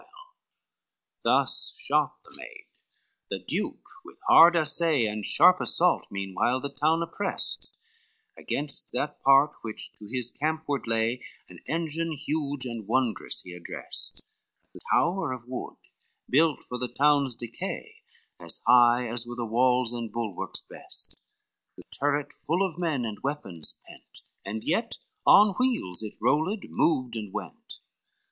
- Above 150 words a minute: No, average, 140 wpm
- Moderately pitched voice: No, low, 130 Hz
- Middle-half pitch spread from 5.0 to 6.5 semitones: Yes, wide, 5.4 semitones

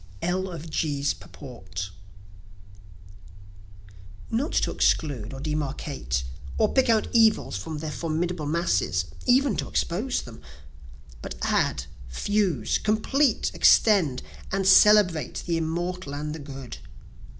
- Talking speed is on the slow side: Yes, slow, 115 wpm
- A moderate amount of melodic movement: No, wide, 6.0 semitones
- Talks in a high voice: No, medium, 160 Hz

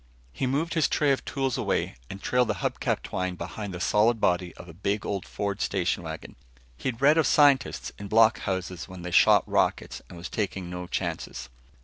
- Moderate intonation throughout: No, wide, 5.8 semitones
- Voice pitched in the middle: No, low, 100 Hz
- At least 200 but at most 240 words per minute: Yes, fast, 205 wpm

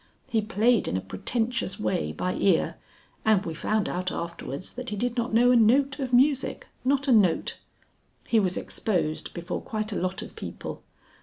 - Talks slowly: No, average, 180 wpm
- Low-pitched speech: No, high, 215 Hz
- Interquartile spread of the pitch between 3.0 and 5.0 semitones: No, wide, 5.4 semitones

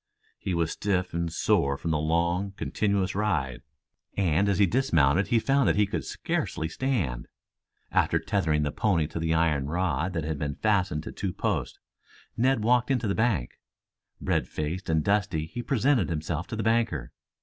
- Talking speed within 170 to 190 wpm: Yes, average, 175 wpm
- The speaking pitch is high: No, very low, 90 Hz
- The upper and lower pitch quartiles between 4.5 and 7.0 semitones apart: Yes, average, 5.1 semitones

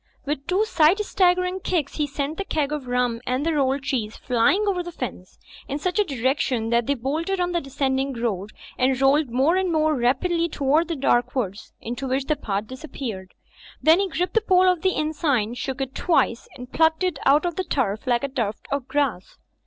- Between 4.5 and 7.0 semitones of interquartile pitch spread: Yes, average, 5.2 semitones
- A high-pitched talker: Yes, very high, 280 Hz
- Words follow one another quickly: Yes, fast, 220 wpm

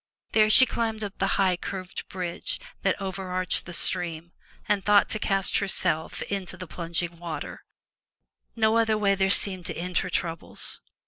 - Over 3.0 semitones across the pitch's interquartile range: No, average, 2.7 semitones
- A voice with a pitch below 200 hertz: Yes, high, 190 Hz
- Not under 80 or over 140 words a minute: No, average, 170 wpm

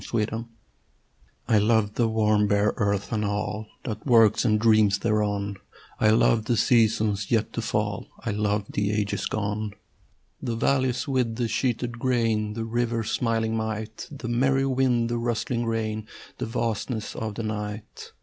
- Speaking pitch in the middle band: No, low, 110 Hz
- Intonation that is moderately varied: No, narrow, 1.9 semitones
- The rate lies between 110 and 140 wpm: No, average, 160 wpm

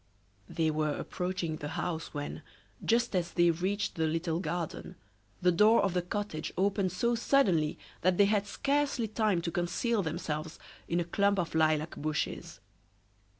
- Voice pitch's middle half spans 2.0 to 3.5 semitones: No, average, 4.1 semitones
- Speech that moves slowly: No, average, 155 wpm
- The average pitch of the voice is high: No, medium, 175 Hz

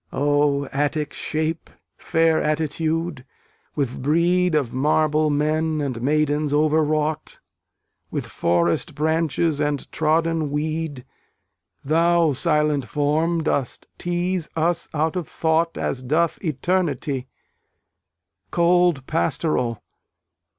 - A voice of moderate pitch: Yes, medium, 155 Hz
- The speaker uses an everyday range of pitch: No, narrow, 2.2 semitones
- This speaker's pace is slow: Yes, slow, 95 wpm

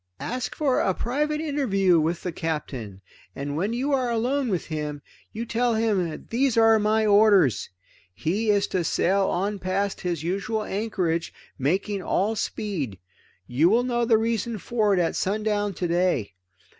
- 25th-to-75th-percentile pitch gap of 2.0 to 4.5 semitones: No, average, 4.9 semitones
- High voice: Yes, high, 200 Hz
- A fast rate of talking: No, average, 155 wpm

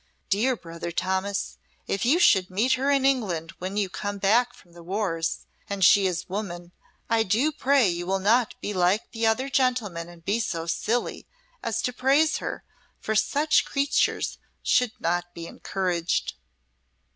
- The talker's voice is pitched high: Yes, high, 200 Hz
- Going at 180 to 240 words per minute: No, average, 170 wpm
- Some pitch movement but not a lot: No, wide, 5.7 semitones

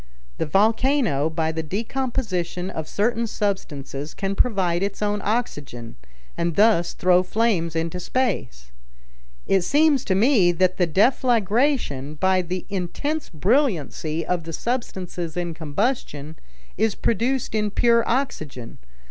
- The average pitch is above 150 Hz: Yes, high, 190 Hz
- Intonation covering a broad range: Yes, wide, 6.0 semitones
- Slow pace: Yes, slow, 125 wpm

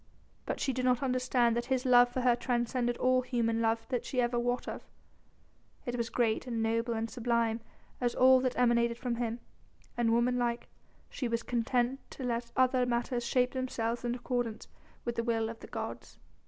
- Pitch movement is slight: Yes, narrow, 1.3 semitones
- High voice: Yes, high, 240 Hz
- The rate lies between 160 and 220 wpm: Yes, average, 180 wpm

